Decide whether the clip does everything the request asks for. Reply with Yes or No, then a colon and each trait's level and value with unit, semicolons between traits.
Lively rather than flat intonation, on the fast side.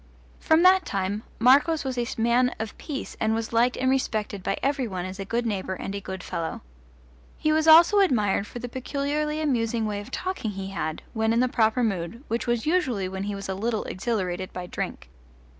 No: average, 5.0 semitones; fast, 210 wpm